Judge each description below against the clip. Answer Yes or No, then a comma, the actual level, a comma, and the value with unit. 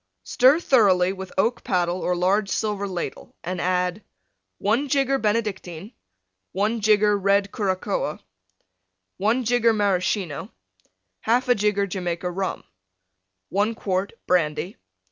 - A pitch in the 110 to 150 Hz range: No, high, 200 Hz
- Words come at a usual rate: No, slow, 110 wpm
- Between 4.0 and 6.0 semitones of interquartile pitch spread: No, average, 3.1 semitones